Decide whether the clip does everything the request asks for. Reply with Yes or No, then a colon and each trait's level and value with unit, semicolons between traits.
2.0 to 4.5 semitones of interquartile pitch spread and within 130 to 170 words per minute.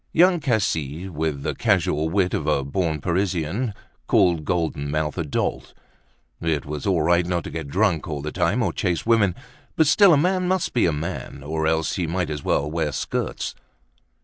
No: average, 4.2 semitones; average, 190 wpm